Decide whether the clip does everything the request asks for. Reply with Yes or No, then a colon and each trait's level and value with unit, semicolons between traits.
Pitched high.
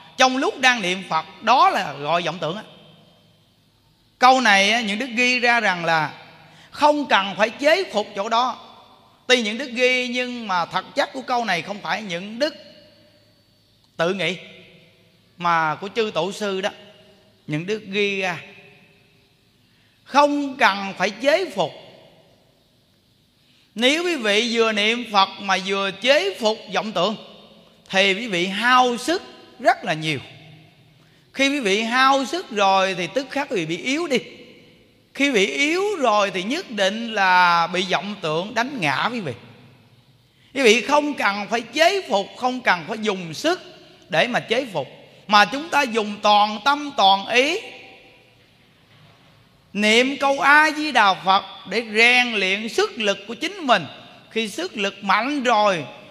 Yes: high, 205 Hz